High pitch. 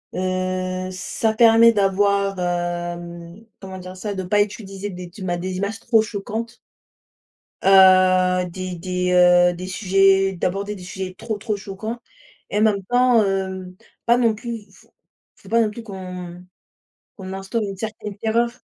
Yes: high, 195 Hz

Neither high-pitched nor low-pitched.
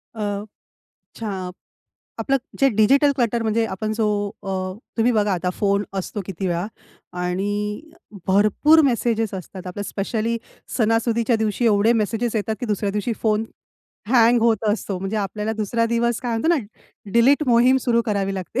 No: high, 220 Hz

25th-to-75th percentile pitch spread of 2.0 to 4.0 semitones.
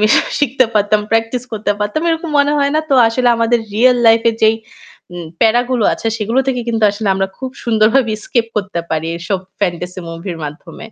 Yes: average, 3.4 semitones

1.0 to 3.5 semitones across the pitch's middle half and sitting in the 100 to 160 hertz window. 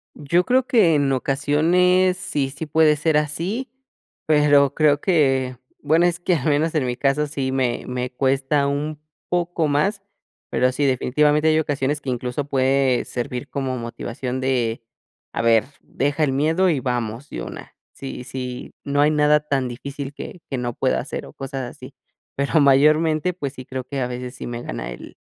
Yes: average, 2.9 semitones; medium, 140 Hz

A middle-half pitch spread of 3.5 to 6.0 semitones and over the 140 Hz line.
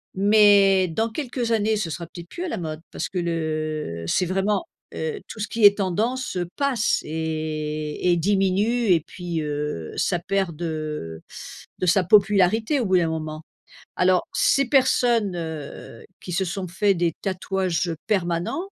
Yes: average, 4.6 semitones; medium, 185 Hz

